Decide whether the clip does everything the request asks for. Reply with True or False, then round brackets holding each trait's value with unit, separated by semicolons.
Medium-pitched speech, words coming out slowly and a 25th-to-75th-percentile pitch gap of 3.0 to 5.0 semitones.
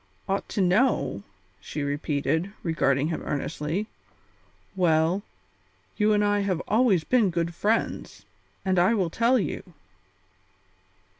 True (180 Hz; 120 wpm; 4.5 semitones)